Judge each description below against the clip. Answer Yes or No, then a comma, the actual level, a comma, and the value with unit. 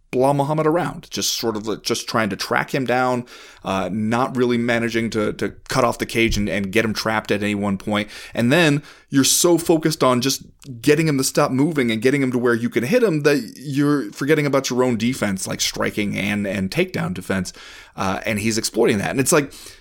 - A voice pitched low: Yes, low, 125 Hz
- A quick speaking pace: Yes, fast, 220 wpm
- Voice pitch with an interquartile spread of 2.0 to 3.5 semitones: No, average, 4.7 semitones